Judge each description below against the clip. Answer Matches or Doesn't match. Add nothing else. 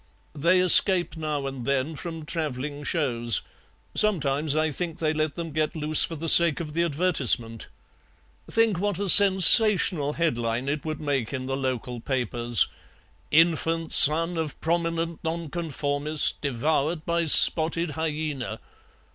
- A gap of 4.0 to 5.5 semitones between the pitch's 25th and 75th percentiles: Doesn't match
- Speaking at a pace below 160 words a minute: Matches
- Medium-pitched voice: Matches